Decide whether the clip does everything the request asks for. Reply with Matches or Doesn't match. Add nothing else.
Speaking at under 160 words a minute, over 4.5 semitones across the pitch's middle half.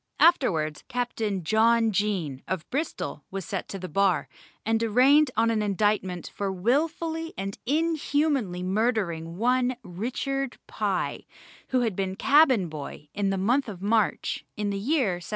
Matches